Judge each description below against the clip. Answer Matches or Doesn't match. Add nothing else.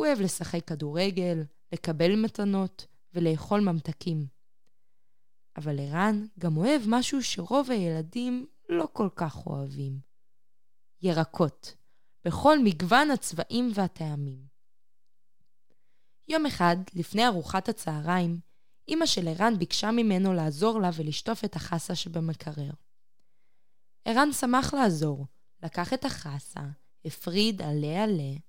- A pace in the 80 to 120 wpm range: Matches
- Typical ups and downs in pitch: Doesn't match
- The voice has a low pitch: Doesn't match